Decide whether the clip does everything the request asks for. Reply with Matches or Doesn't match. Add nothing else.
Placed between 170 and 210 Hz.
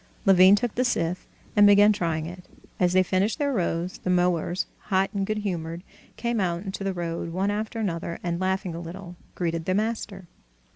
Matches